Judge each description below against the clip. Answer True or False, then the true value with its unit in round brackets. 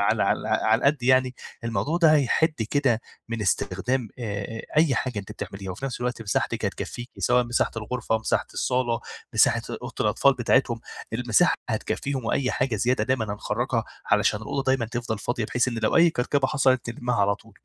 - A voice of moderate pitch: False (120 Hz)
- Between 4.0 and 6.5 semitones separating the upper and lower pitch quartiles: False (3.0 semitones)